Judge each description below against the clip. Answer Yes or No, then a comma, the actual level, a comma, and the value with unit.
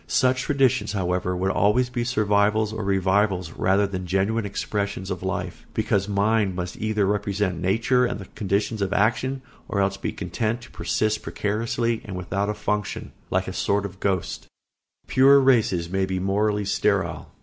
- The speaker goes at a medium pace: Yes, average, 170 wpm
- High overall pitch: No, low, 100 Hz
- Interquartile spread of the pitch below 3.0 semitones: Yes, narrow, 2.4 semitones